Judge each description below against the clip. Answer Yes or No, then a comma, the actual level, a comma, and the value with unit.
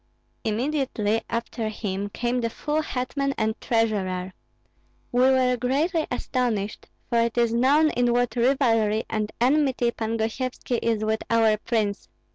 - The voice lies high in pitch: Yes, high, 235 Hz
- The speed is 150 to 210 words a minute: No, slow, 135 wpm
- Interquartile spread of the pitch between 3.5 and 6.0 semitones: No, average, 2.7 semitones